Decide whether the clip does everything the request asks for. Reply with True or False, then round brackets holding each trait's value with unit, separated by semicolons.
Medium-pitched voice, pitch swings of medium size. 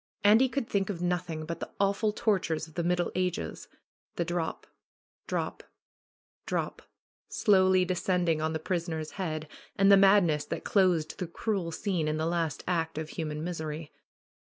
True (175 Hz; 3.2 semitones)